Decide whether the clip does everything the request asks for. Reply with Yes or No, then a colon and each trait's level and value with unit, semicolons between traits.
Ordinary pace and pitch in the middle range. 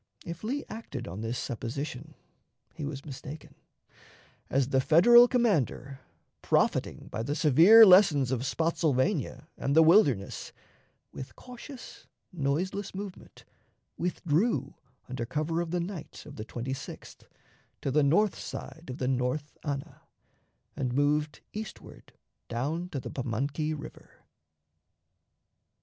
No: slow, 120 wpm; medium, 150 Hz